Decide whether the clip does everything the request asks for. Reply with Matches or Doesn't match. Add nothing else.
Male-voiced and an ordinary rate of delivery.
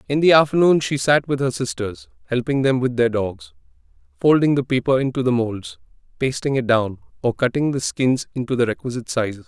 Matches